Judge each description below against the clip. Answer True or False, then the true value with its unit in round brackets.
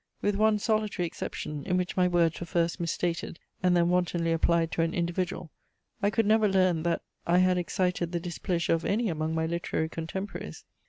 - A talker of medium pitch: True (175 Hz)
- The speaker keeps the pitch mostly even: True (1.9 semitones)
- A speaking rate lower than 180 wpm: False (190 wpm)